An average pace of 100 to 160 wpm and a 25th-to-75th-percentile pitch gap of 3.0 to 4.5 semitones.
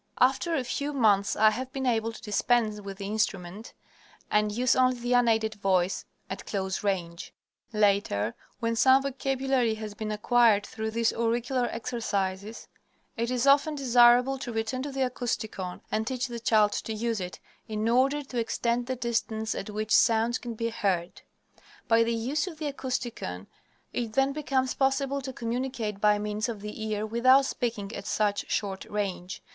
No: average, 170 wpm; average, 3.3 semitones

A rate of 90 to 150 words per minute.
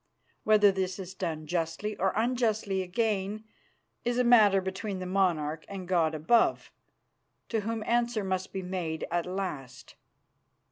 Yes: average, 140 wpm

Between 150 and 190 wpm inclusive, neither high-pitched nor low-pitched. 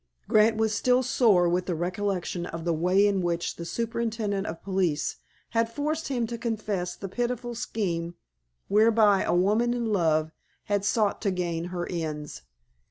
No: average, 165 wpm; high, 200 Hz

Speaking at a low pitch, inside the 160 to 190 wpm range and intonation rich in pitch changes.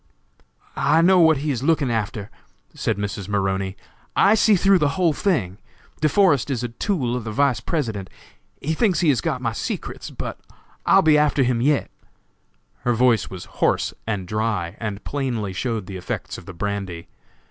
Yes: low, 120 Hz; average, 180 wpm; wide, 6.7 semitones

